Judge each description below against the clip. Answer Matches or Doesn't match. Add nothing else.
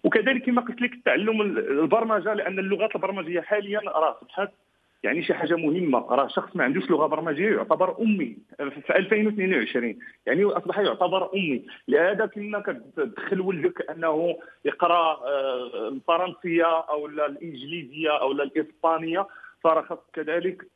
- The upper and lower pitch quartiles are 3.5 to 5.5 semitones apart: Matches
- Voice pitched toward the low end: Doesn't match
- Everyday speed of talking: Doesn't match